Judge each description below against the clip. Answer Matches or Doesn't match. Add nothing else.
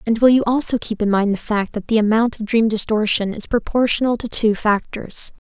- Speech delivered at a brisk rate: Matches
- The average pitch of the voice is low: Doesn't match